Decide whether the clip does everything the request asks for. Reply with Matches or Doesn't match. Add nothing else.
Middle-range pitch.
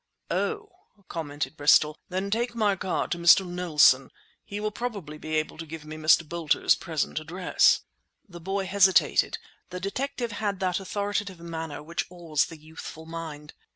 Matches